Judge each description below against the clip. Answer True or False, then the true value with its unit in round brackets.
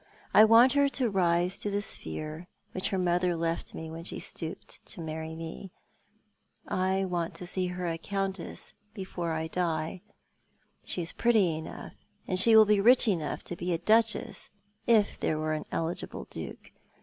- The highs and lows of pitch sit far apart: False (3.5 semitones)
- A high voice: False (180 Hz)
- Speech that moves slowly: False (175 wpm)